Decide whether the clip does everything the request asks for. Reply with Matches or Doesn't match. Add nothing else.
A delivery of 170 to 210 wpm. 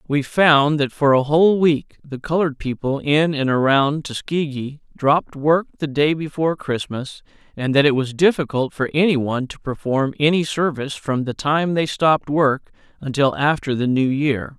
Matches